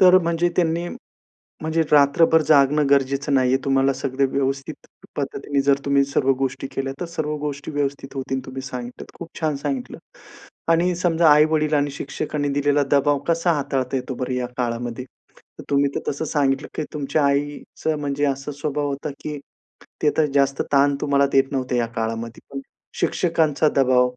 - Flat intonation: Yes, narrow, 2.0 semitones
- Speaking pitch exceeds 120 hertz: Yes, medium, 140 Hz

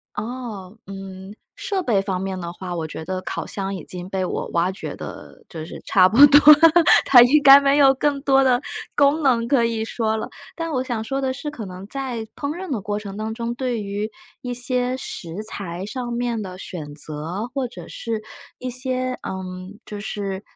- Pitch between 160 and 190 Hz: No, high, 220 Hz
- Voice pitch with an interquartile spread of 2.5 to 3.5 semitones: No, average, 5.2 semitones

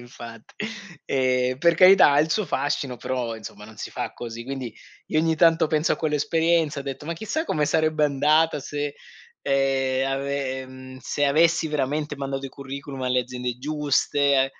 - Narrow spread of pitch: No, average, 3.0 semitones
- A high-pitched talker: No, medium, 140 Hz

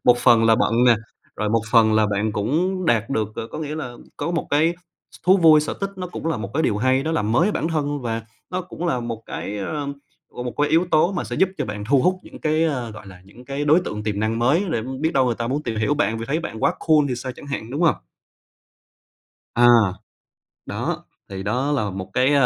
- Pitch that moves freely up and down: Yes, wide, 5.8 semitones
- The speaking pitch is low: Yes, low, 130 Hz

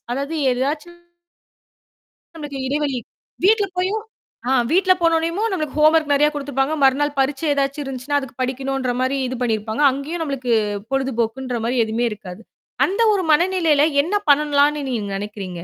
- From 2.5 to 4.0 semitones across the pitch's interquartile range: Yes, average, 3.4 semitones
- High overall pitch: Yes, very high, 280 Hz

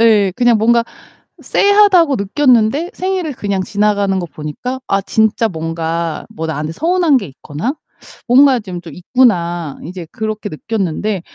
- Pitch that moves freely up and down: Yes, wide, 6.9 semitones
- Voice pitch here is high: Yes, high, 210 Hz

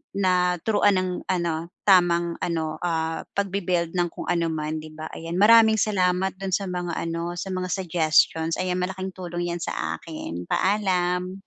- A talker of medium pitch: Yes, medium, 180 Hz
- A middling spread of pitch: No, narrow, 2.1 semitones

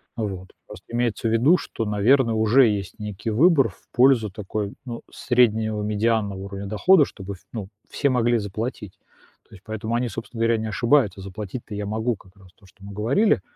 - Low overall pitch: Yes, low, 110 Hz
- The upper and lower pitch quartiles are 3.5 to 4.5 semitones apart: No, average, 2.9 semitones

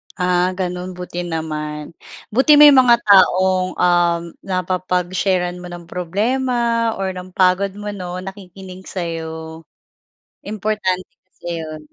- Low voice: No, medium, 185 Hz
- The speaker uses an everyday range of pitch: No, narrow, 2.0 semitones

